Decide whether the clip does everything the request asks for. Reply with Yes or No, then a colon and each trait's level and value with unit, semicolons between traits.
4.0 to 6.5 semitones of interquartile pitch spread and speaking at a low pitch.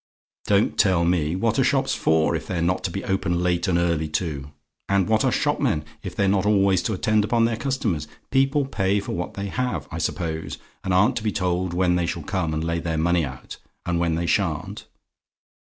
No: average, 3.2 semitones; very low, 90 Hz